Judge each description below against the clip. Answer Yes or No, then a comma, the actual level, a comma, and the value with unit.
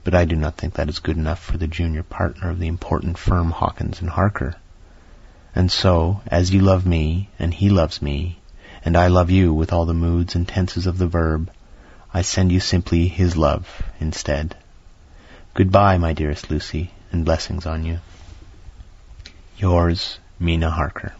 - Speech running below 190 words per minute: Yes, average, 175 wpm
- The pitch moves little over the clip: Yes, narrow, 2.1 semitones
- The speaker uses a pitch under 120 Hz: Yes, very low, 85 Hz